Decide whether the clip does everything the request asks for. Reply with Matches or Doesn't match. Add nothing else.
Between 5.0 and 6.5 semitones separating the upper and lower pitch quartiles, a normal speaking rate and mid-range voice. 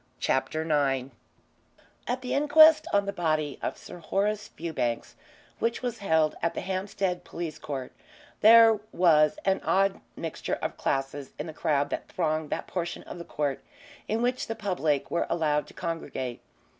Matches